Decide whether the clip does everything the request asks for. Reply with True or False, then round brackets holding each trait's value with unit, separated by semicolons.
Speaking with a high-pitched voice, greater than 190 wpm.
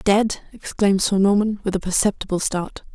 False (200 Hz; 165 wpm)